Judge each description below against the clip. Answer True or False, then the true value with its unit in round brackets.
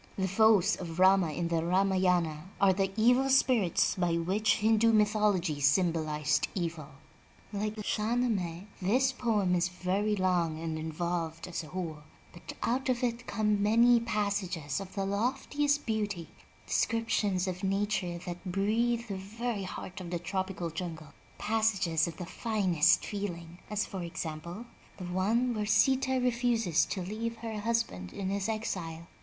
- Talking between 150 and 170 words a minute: True (155 wpm)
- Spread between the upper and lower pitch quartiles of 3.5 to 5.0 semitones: True (4.2 semitones)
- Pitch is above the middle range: True (195 Hz)